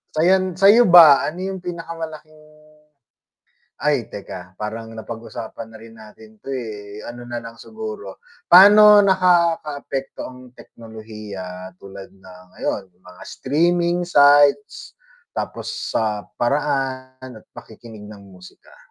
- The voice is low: Yes, low, 125 Hz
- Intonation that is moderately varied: No, wide, 7.3 semitones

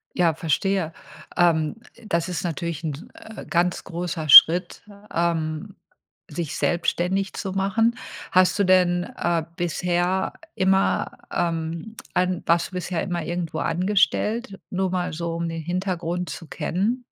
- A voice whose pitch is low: No, medium, 175 Hz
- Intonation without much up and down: Yes, narrow, 2.2 semitones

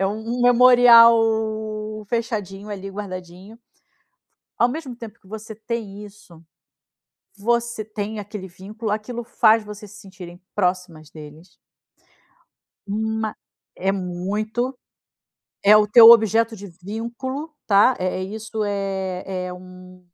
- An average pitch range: Yes, average, 3.4 semitones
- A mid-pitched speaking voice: No, high, 210 Hz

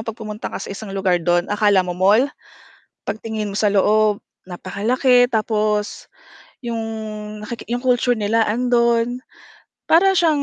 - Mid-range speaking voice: No, high, 215 Hz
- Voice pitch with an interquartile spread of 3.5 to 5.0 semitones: No, average, 2.9 semitones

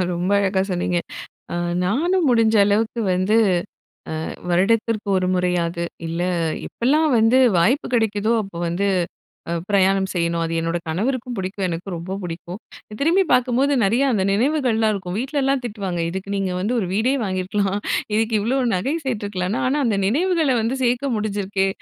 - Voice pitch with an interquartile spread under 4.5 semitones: No, average, 4.8 semitones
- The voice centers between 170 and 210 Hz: Yes, high, 205 Hz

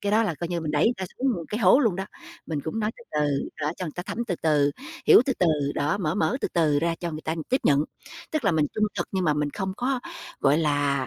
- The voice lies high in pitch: No, medium, 170 Hz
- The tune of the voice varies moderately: No, wide, 5.8 semitones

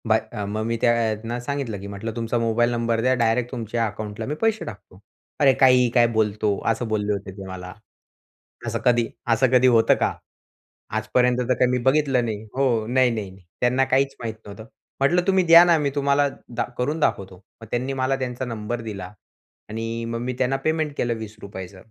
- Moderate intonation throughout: Yes, average, 3.0 semitones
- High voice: No, low, 115 Hz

